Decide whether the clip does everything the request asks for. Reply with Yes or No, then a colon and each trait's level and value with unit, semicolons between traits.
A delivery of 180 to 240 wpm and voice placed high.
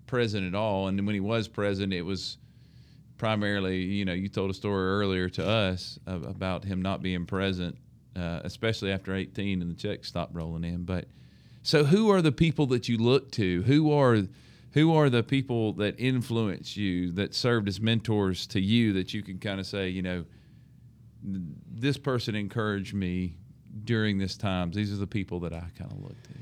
No: average, 195 wpm; low, 100 Hz